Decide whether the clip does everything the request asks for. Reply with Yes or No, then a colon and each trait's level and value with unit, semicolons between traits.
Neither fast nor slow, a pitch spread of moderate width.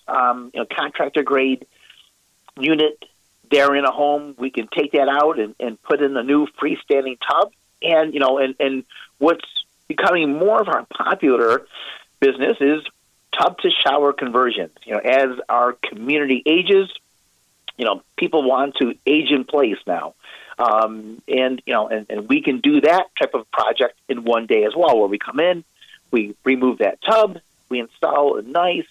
Yes: average, 175 wpm; average, 3.7 semitones